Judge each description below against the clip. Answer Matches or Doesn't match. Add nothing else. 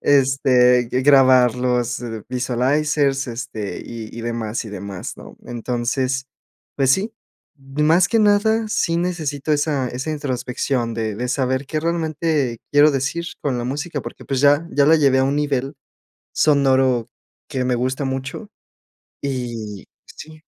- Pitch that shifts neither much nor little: Matches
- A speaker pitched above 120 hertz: Matches